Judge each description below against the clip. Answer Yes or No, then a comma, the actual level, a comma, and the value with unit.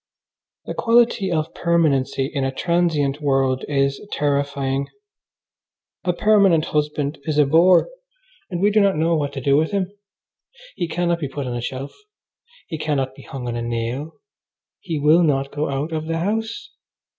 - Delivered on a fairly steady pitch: No, average, 3.9 semitones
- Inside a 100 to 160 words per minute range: No, average, 170 wpm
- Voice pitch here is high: No, medium, 150 Hz